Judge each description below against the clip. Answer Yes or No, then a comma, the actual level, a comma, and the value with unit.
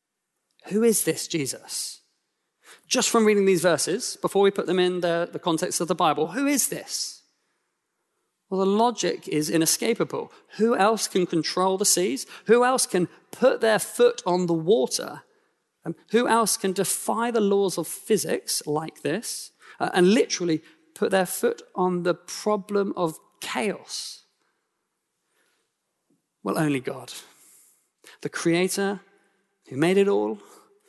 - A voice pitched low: No, high, 195 Hz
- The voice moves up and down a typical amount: Yes, average, 4.7 semitones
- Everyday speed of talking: Yes, average, 145 wpm